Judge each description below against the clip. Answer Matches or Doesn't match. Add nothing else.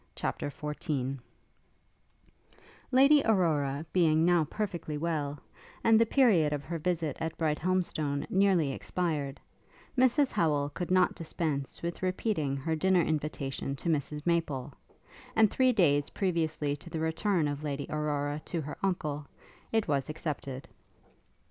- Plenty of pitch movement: Doesn't match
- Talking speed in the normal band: Doesn't match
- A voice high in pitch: Doesn't match